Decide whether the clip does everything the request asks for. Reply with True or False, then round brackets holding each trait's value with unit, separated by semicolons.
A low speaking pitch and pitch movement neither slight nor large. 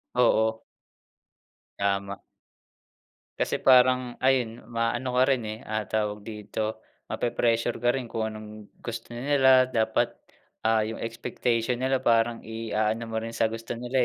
False (115 Hz; 1.9 semitones)